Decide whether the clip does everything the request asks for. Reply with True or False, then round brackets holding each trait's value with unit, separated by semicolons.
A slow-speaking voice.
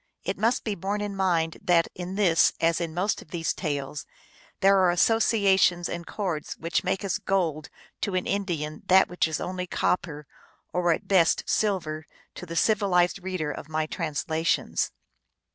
False (165 wpm)